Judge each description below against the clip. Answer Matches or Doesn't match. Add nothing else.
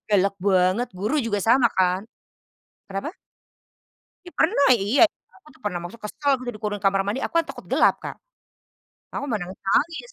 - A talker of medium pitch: Doesn't match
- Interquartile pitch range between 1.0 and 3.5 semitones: Doesn't match